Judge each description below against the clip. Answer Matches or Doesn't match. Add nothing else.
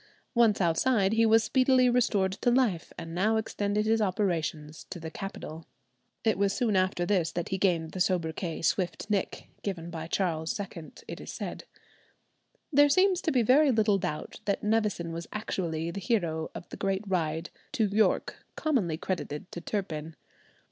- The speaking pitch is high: Matches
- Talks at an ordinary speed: Matches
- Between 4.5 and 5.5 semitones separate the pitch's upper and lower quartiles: Matches